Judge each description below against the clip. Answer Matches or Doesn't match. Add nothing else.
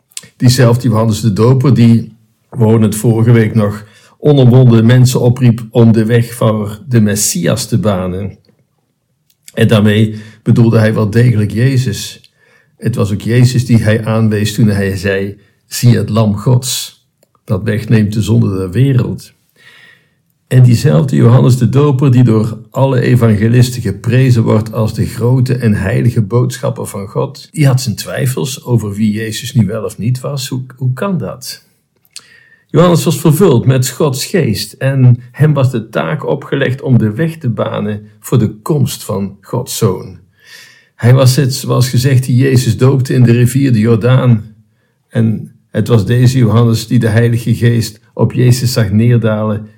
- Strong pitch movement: Doesn't match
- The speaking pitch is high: Doesn't match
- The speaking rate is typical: Matches